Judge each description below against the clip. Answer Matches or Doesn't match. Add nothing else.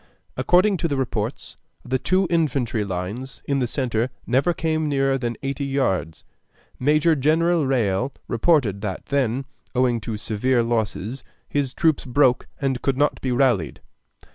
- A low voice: Matches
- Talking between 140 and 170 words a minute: Matches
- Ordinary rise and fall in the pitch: Matches